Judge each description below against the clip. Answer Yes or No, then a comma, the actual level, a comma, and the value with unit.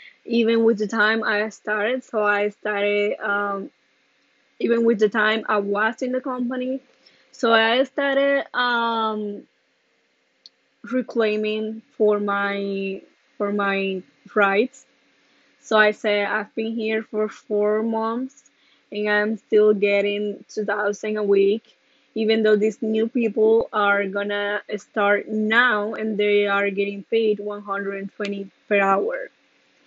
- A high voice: Yes, high, 215 Hz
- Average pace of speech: No, slow, 125 wpm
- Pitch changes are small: Yes, narrow, 1.9 semitones